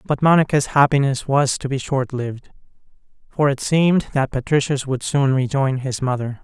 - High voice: No, low, 135 Hz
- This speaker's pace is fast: No, average, 160 wpm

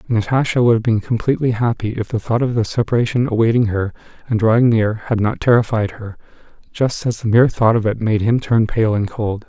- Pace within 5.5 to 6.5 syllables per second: Yes, 5.8 syllables/s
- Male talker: Yes, male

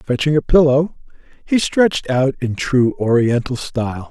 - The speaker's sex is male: Yes, male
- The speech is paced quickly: No, average, 145 wpm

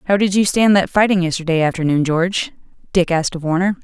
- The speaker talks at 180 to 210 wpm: Yes, fast, 205 wpm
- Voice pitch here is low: No, medium, 180 Hz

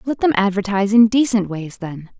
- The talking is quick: No, average, 190 wpm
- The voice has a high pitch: Yes, high, 210 Hz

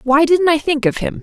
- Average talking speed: No, fast, 295 wpm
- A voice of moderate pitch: No, very high, 300 Hz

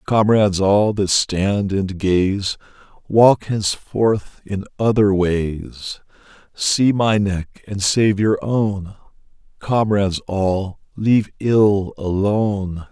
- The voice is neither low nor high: No, low, 100 Hz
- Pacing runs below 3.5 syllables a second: Yes, 3.1 syllables/s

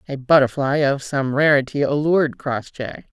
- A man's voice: No, female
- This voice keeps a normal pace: No, slow, 130 wpm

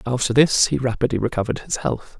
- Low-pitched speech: Yes, low, 120 Hz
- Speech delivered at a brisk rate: No, average, 190 wpm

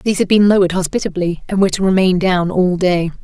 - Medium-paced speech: No, fast, 220 wpm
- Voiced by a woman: Yes, female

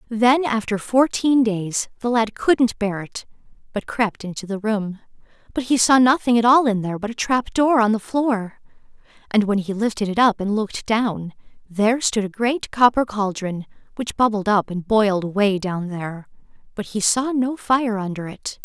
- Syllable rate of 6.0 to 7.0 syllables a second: No, 4.8 syllables/s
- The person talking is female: Yes, female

